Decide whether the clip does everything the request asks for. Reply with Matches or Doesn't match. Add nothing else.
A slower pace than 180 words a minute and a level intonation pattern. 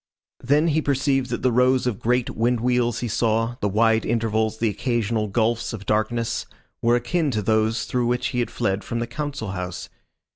Doesn't match